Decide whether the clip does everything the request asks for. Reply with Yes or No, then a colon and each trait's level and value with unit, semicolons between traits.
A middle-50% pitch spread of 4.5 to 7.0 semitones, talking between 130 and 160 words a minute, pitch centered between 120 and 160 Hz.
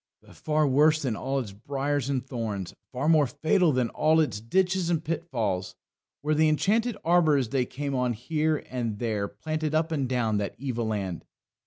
No: average, 5.0 semitones; average, 180 wpm; medium, 140 Hz